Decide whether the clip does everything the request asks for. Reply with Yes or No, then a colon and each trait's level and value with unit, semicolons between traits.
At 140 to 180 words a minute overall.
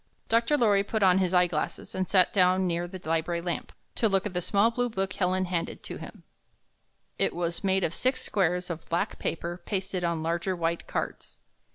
No: average, 200 wpm